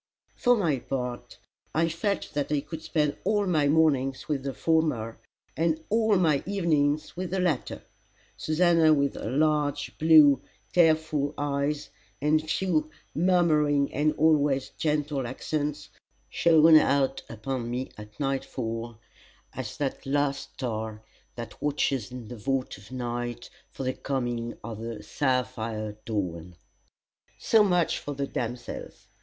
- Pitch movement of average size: Yes, average, 4.0 semitones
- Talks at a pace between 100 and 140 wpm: Yes, slow, 135 wpm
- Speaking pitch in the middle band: Yes, medium, 145 Hz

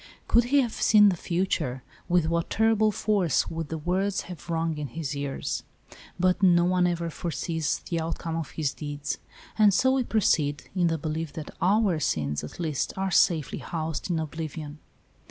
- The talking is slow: No, average, 175 wpm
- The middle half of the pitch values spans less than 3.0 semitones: No, average, 3.4 semitones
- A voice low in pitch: No, medium, 165 Hz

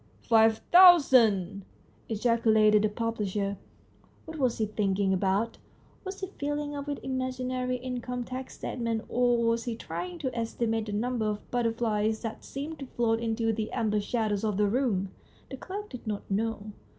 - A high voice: Yes, high, 230 Hz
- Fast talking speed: No, average, 170 wpm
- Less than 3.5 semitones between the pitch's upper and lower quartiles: Yes, average, 3.1 semitones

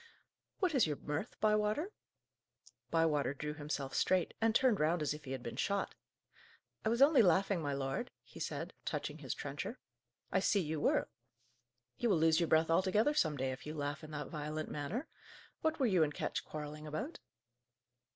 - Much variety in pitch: Yes, wide, 6.1 semitones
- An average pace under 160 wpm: No, average, 180 wpm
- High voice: No, medium, 160 Hz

